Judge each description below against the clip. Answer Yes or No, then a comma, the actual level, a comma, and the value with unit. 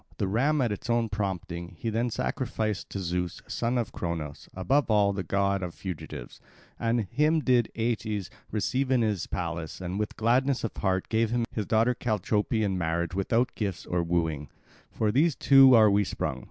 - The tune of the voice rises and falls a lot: No, average, 4.5 semitones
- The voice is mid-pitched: No, low, 105 Hz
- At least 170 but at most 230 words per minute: Yes, average, 180 wpm